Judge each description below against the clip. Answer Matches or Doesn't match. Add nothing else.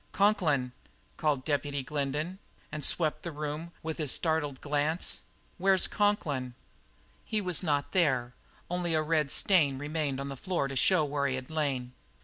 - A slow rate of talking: Doesn't match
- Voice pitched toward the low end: Doesn't match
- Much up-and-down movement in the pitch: Doesn't match